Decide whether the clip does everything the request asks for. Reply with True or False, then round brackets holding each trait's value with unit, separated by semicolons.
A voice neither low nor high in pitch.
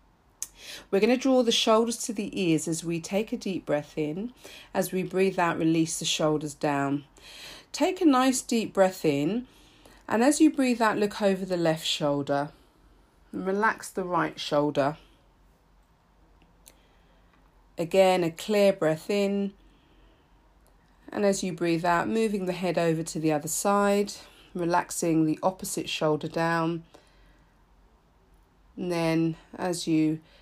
True (170 Hz)